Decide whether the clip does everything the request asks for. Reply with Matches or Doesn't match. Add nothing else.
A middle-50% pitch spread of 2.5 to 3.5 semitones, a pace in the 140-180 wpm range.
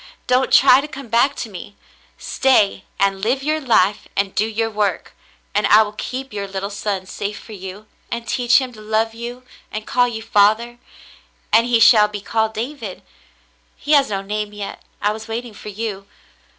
Doesn't match